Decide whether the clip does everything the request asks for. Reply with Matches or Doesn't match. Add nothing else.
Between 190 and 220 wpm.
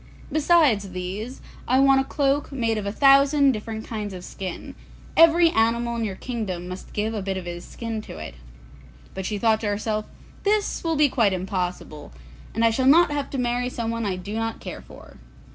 Matches